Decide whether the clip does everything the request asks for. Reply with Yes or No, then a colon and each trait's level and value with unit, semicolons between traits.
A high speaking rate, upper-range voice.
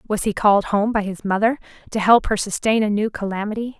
Yes: fast, 220 wpm; high, 210 Hz